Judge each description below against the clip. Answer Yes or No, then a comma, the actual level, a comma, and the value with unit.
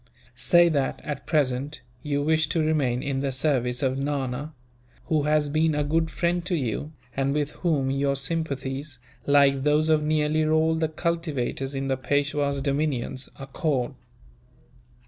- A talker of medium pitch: Yes, medium, 145 Hz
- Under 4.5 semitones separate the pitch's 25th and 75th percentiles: Yes, narrow, 2.5 semitones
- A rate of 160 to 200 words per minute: No, average, 150 wpm